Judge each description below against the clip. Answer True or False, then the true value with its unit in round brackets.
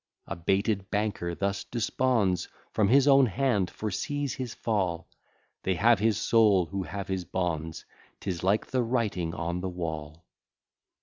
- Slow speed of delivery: False (145 wpm)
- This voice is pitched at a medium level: False (100 Hz)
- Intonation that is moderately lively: True (4.4 semitones)